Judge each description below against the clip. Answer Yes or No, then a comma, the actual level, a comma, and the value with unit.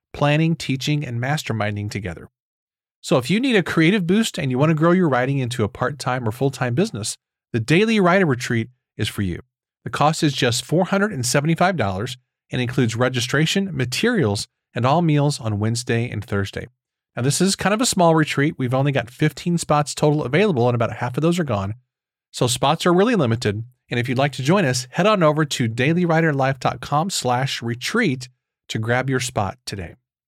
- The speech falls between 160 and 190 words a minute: Yes, average, 180 wpm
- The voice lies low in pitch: Yes, low, 130 Hz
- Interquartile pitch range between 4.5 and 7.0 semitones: Yes, average, 4.9 semitones